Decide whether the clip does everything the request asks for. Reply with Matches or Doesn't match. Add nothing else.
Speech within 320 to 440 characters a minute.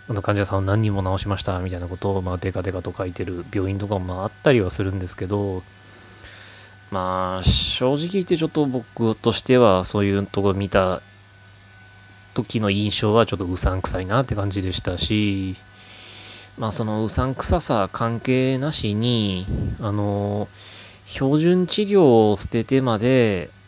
Doesn't match